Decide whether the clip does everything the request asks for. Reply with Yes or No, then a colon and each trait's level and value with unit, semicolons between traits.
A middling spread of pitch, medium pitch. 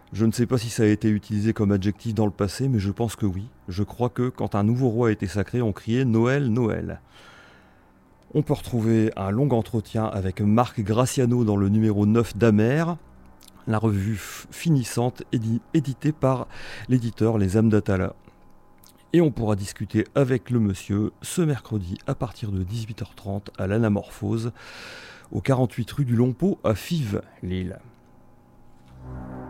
No: average, 3.3 semitones; low, 110 Hz